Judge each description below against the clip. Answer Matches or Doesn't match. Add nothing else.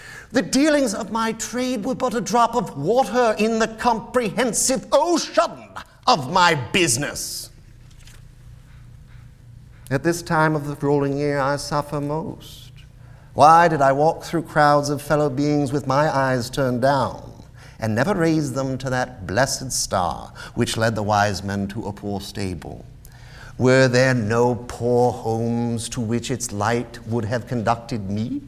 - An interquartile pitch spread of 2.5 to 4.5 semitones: Doesn't match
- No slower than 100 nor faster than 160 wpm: Matches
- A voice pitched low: Matches